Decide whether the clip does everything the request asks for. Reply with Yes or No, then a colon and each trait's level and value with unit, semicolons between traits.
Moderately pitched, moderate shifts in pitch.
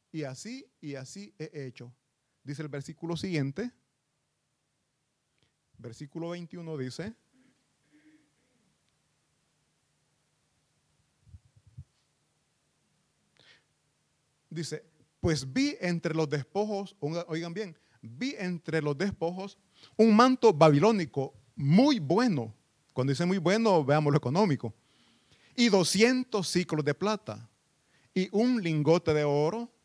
No: medium, 165 Hz; wide, 5.7 semitones